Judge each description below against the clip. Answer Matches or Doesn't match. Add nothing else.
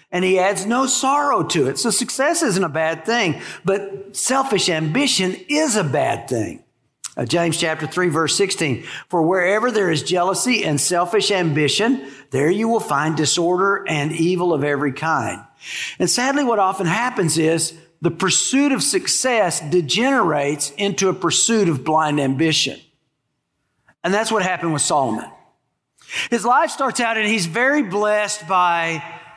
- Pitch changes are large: Matches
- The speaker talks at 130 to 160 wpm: Matches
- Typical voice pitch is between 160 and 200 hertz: Matches